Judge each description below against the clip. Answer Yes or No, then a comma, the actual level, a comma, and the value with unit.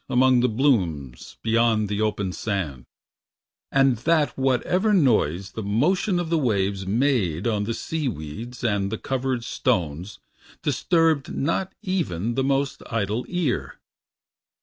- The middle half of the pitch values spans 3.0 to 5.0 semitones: No, wide, 5.5 semitones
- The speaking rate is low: Yes, slow, 130 wpm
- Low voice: Yes, low, 120 Hz